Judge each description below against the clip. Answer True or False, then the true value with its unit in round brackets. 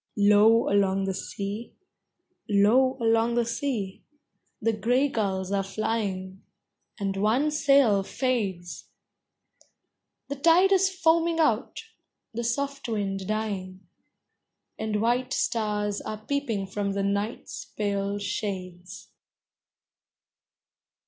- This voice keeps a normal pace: False (100 wpm)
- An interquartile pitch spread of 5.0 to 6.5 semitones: False (3.9 semitones)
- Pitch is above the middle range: True (215 Hz)